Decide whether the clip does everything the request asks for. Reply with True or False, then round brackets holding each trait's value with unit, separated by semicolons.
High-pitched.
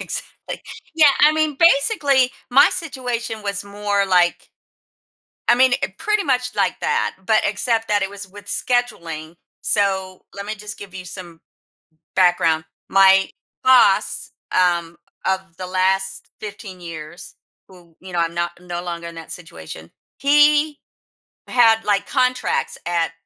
True (200 Hz)